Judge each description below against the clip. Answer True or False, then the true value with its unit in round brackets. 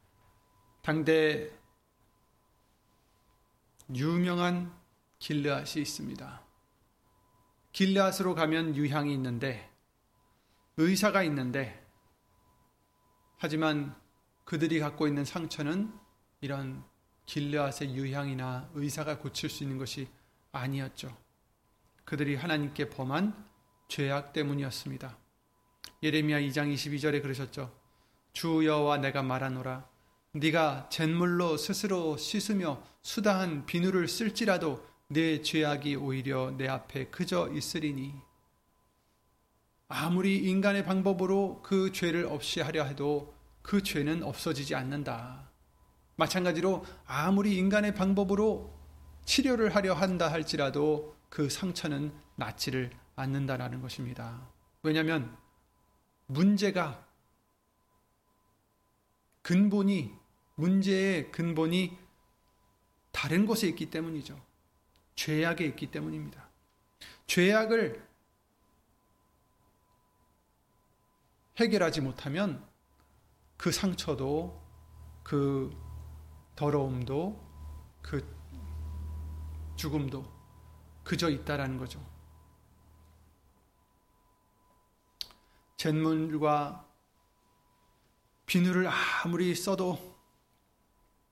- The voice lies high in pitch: False (145 Hz)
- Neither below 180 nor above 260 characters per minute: True (195 characters per minute)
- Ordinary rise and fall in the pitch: False (5.8 semitones)